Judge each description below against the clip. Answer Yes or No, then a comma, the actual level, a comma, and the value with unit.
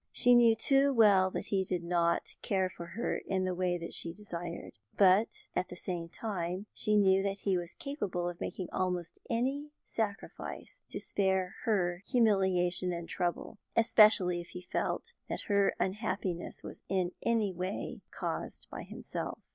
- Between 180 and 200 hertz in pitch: Yes, high, 190 Hz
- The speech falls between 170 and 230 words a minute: No, average, 160 wpm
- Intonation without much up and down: No, average, 3.2 semitones